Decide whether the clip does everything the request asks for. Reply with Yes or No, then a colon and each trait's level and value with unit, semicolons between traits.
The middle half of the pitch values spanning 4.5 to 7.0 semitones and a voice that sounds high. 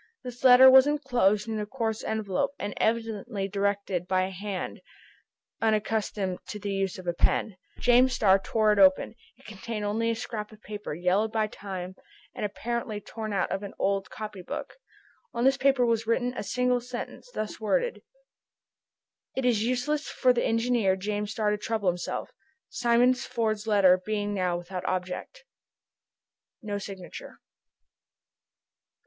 No: average, 3.4 semitones; high, 215 Hz